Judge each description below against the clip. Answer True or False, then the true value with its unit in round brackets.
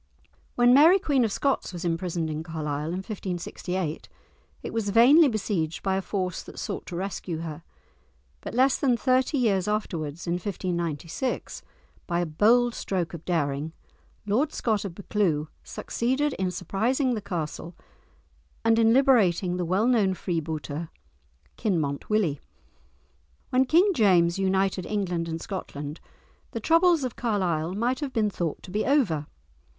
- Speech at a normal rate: True (145 wpm)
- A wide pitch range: True (5.9 semitones)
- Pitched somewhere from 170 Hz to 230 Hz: True (190 Hz)